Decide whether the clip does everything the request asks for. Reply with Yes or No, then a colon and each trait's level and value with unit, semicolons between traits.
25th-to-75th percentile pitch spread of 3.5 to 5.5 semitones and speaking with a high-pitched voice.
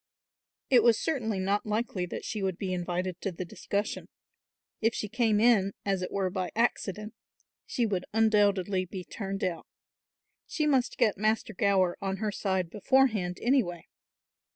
No: average, 3.0 semitones; high, 200 Hz